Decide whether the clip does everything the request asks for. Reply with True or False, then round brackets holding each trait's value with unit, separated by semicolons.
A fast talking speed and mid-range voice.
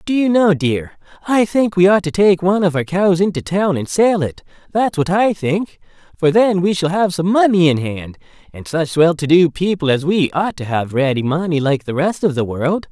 True (235 wpm; 170 Hz)